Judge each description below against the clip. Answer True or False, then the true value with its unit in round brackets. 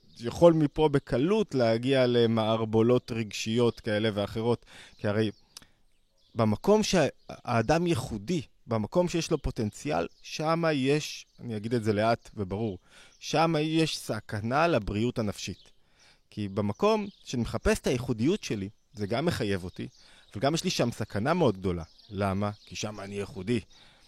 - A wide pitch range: True (5.9 semitones)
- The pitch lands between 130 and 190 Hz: False (115 Hz)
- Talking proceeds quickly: False (130 wpm)